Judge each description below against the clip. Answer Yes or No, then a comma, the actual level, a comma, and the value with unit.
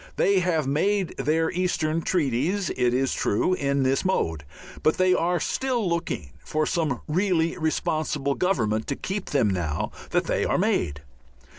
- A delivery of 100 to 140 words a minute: No, average, 155 wpm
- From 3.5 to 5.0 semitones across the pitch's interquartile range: No, wide, 5.6 semitones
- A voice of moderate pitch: Yes, medium, 155 Hz